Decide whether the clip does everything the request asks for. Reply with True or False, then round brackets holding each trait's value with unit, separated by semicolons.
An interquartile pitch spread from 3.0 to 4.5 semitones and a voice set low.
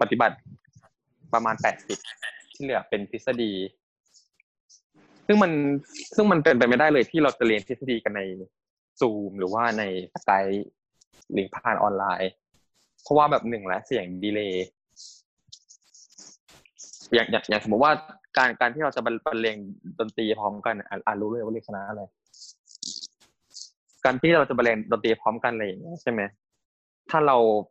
True (4.1 semitones; 115 Hz)